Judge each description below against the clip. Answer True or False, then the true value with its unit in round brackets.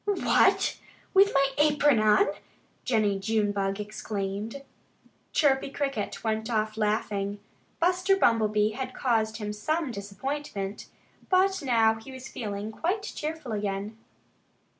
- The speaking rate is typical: False (115 wpm)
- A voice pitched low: False (225 Hz)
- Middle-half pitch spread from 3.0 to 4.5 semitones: False (5.4 semitones)